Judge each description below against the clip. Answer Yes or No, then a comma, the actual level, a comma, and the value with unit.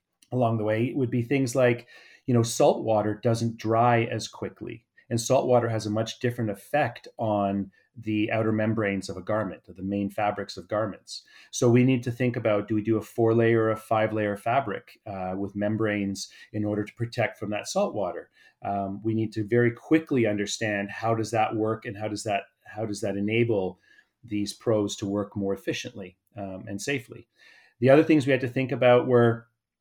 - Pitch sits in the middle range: No, low, 110 Hz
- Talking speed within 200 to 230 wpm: Yes, fast, 205 wpm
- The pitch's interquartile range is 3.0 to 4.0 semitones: No, narrow, 2.4 semitones